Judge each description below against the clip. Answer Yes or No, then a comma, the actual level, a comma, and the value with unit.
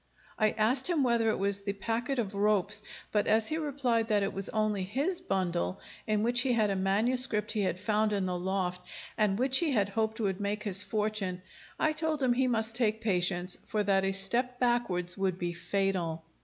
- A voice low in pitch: No, high, 210 Hz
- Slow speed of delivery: No, fast, 205 wpm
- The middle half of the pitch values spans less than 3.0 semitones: No, average, 3.7 semitones